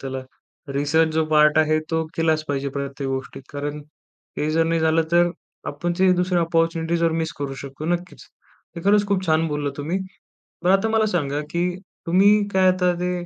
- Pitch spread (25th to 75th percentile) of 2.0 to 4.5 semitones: Yes, average, 3.2 semitones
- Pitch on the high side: No, medium, 160 Hz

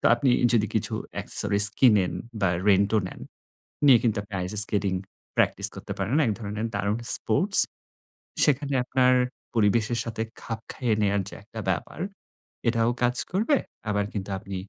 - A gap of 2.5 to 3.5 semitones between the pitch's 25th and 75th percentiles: Yes, average, 3.1 semitones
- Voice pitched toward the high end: No, low, 110 Hz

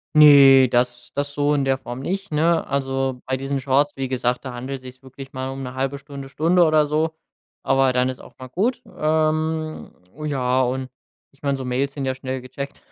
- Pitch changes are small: Yes, narrow, 2.3 semitones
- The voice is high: No, low, 135 Hz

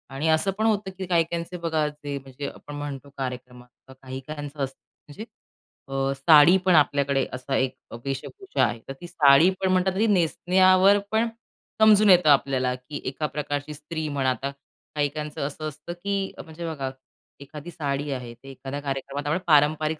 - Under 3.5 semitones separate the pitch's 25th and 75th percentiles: No, average, 4.0 semitones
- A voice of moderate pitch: Yes, medium, 150 Hz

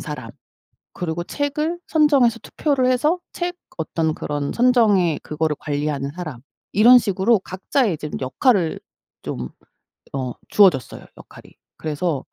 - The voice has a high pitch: No, medium, 180 Hz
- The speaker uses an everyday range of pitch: No, wide, 8.8 semitones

